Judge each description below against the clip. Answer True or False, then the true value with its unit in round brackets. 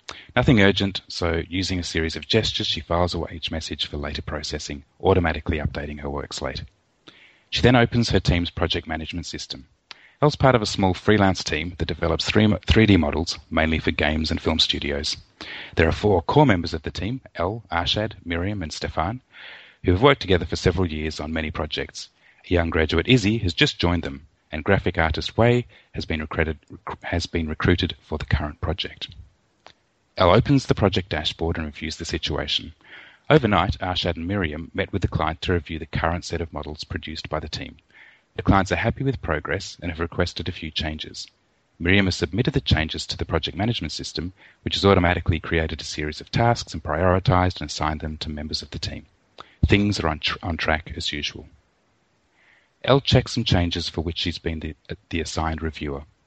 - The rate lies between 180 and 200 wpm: True (190 wpm)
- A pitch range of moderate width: True (3.9 semitones)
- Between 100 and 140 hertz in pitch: False (85 Hz)